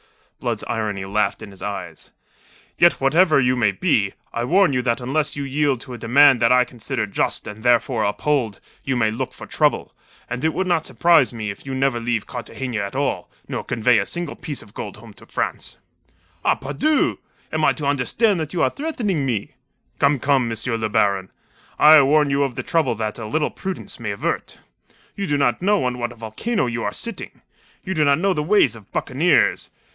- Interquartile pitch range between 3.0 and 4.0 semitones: No, average, 5.2 semitones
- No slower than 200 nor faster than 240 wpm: Yes, fast, 205 wpm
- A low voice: Yes, low, 130 Hz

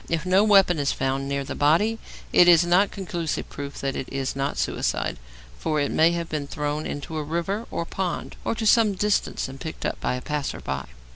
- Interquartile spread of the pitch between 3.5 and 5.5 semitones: Yes, average, 4.6 semitones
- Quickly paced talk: Yes, fast, 215 wpm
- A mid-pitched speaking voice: Yes, medium, 160 Hz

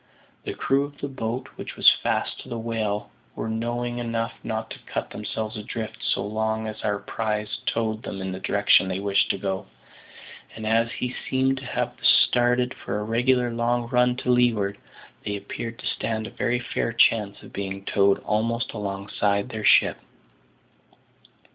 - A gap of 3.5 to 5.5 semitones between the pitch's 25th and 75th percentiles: No, average, 2.7 semitones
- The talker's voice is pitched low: Yes, low, 110 Hz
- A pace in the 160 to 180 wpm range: Yes, average, 175 wpm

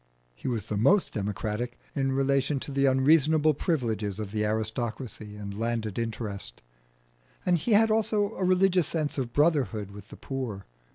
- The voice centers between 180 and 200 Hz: No, low, 130 Hz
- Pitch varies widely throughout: Yes, wide, 6.3 semitones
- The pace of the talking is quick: No, average, 160 wpm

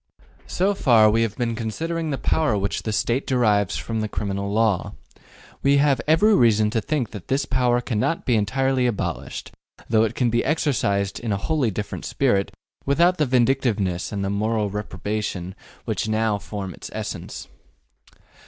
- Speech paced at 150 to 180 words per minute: Yes, average, 165 wpm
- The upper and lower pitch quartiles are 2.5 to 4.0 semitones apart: No, average, 4.4 semitones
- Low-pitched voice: Yes, low, 115 Hz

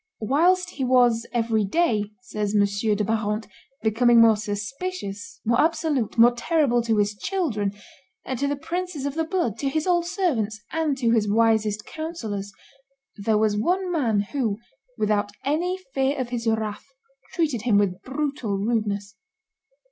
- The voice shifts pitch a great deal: Yes, wide, 5.9 semitones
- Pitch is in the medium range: No, high, 230 Hz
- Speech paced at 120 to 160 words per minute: Yes, average, 150 wpm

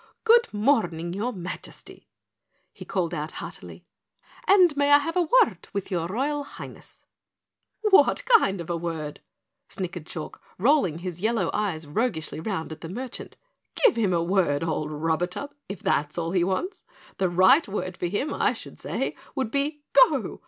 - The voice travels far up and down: Yes, wide, 8.8 semitones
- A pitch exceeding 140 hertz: Yes, high, 190 Hz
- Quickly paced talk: No, average, 165 wpm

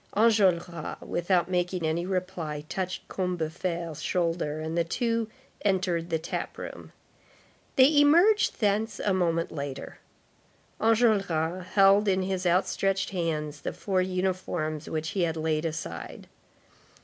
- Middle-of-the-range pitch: Yes, medium, 180 Hz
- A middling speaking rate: No, slow, 125 wpm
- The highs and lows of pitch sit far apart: No, average, 3.2 semitones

